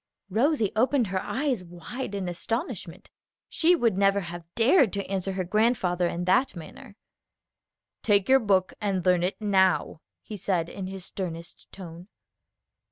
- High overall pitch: Yes, high, 195 Hz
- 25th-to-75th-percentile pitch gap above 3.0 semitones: Yes, average, 3.9 semitones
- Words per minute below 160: Yes, average, 150 wpm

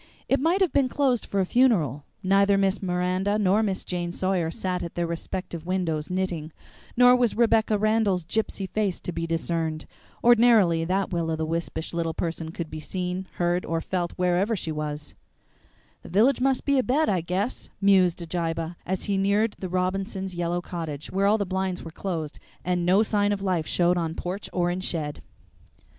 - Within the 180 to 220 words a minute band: Yes, average, 185 wpm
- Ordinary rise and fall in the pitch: Yes, average, 3.2 semitones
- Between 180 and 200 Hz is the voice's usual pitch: Yes, medium, 185 Hz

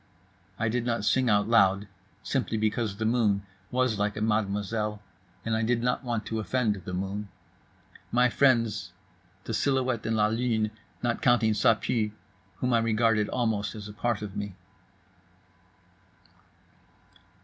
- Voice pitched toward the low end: Yes, low, 110 Hz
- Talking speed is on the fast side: No, average, 150 wpm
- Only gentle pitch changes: Yes, narrow, 2.3 semitones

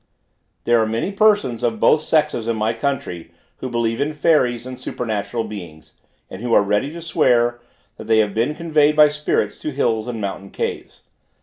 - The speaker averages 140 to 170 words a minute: No, average, 185 wpm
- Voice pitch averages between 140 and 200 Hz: No, low, 120 Hz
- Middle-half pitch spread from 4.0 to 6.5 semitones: Yes, average, 5.2 semitones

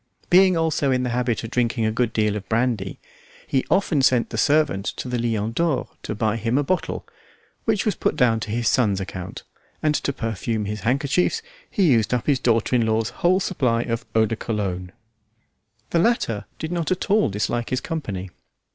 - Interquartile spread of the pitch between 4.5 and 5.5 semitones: Yes, average, 5.0 semitones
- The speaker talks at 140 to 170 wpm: No, average, 195 wpm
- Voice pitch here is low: Yes, low, 120 Hz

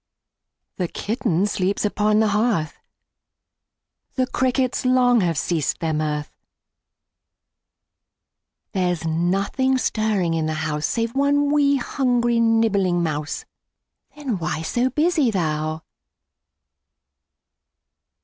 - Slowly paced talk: Yes, slow, 100 wpm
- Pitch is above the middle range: Yes, high, 210 Hz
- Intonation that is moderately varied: No, wide, 7.3 semitones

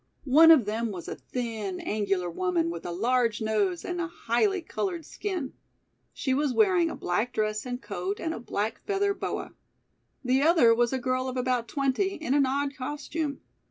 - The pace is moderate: Yes, average, 185 wpm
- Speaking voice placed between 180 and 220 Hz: No, very high, 255 Hz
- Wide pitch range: Yes, wide, 6.6 semitones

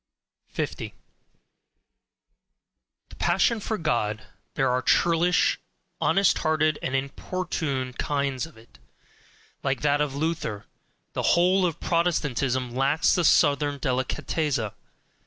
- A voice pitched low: No, medium, 145 Hz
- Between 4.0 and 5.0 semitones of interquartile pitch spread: Yes, average, 4.3 semitones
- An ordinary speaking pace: No, slow, 105 wpm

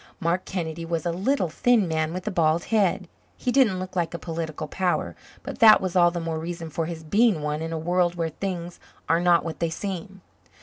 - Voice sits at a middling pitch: Yes, medium, 175 Hz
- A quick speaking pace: Yes, fast, 220 wpm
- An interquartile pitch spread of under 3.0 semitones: Yes, narrow, 2.4 semitones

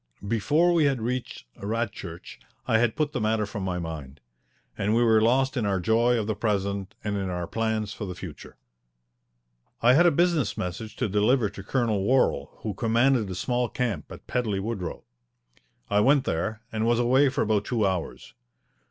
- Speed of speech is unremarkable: Yes, average, 185 wpm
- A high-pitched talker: No, low, 110 Hz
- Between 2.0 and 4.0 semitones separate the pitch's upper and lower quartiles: Yes, average, 3.7 semitones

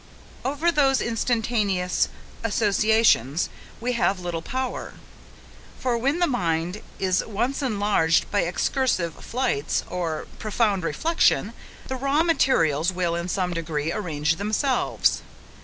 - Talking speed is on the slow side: Yes, slow, 115 wpm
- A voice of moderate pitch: No, high, 205 Hz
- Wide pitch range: Yes, wide, 6.8 semitones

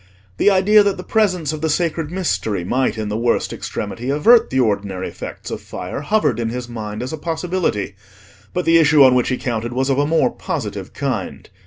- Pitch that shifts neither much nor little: No, wide, 6.6 semitones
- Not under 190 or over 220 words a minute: Yes, fast, 205 wpm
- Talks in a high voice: No, medium, 140 Hz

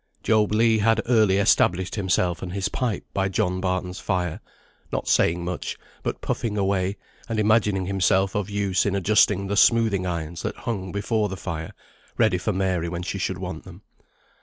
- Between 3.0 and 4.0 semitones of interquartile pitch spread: No, narrow, 2.5 semitones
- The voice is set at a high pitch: No, very low, 95 Hz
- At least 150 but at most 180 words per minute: Yes, average, 175 wpm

